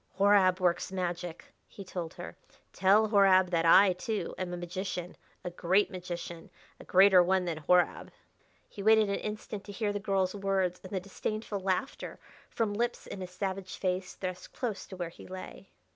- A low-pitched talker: No, high, 190 Hz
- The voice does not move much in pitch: Yes, narrow, 2.0 semitones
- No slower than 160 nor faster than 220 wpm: Yes, average, 175 wpm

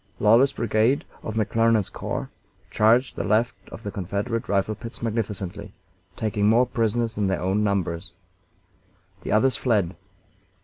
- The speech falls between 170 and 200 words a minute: No, slow, 135 wpm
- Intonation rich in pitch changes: No, narrow, 2.4 semitones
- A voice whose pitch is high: No, low, 110 Hz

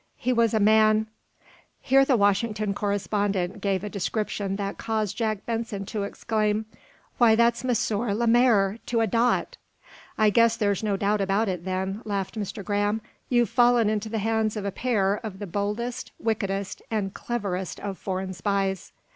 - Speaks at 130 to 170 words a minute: Yes, average, 165 wpm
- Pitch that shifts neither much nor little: No, narrow, 2.3 semitones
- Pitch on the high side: Yes, high, 210 Hz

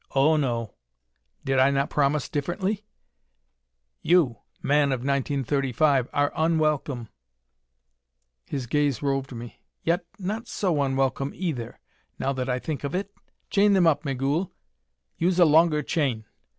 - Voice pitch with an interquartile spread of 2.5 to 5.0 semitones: Yes, average, 3.5 semitones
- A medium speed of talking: No, slow, 130 wpm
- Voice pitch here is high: No, medium, 145 Hz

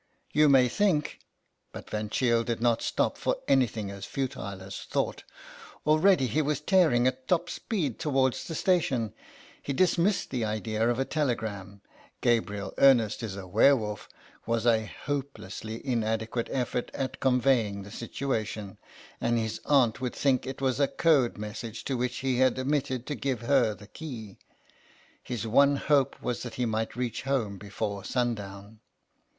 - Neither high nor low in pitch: No, low, 120 Hz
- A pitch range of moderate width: Yes, average, 3.9 semitones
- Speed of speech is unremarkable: Yes, average, 170 wpm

